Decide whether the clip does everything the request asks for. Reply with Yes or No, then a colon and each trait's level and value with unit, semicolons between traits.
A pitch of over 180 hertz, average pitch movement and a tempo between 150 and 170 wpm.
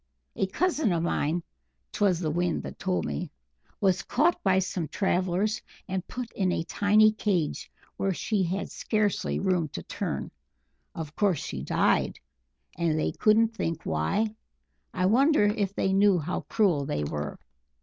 Yes: high, 190 Hz; average, 3.9 semitones; average, 155 wpm